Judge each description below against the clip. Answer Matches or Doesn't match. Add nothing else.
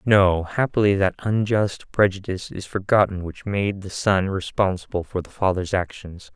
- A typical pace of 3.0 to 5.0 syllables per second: Matches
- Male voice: Matches